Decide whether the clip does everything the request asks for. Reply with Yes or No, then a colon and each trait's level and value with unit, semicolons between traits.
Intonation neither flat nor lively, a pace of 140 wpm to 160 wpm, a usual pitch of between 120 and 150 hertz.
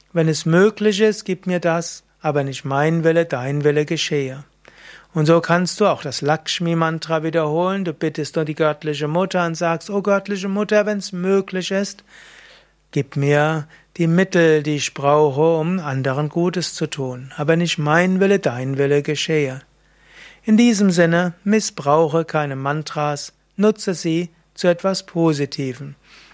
No: average, 3.6 semitones; average, 155 wpm; medium, 165 Hz